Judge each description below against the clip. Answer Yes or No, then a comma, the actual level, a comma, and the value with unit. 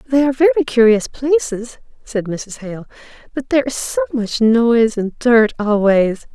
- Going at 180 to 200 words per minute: No, average, 160 wpm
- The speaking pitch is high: Yes, high, 230 Hz